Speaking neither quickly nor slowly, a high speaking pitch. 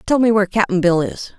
No: fast, 260 wpm; high, 210 Hz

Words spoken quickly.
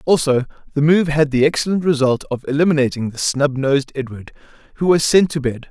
No: average, 190 wpm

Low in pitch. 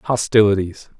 Yes: low, 105 Hz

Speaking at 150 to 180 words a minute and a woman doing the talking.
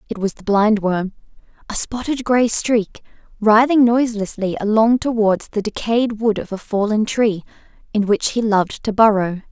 Yes: average, 160 wpm; female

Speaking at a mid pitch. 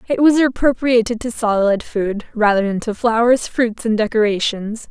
No: high, 225 Hz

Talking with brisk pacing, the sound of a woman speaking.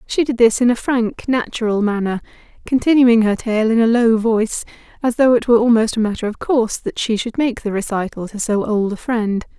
Yes: fast, 220 wpm; female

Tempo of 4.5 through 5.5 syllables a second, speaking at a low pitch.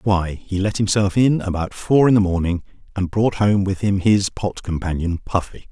Yes: 4.8 syllables/s; low, 100 Hz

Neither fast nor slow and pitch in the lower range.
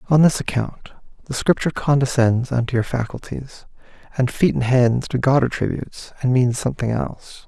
Yes: average, 160 wpm; low, 130 Hz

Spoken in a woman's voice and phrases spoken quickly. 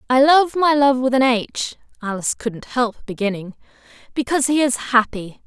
No: female; average, 165 wpm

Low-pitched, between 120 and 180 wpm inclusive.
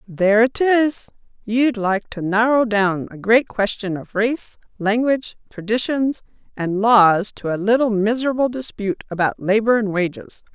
No: high, 220 Hz; average, 150 wpm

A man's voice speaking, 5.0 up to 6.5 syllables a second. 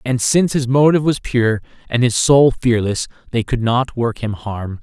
No: male; 4.8 syllables/s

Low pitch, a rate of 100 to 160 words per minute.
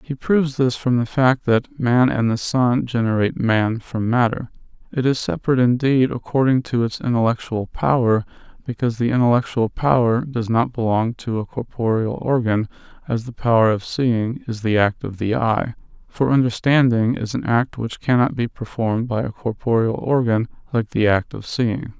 No: low, 120 Hz; average, 175 wpm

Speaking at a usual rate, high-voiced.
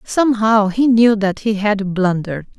Yes: average, 160 wpm; high, 210 Hz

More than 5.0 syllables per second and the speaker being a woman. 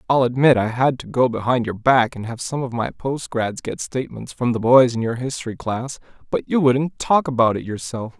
No: 5.2 syllables/s; male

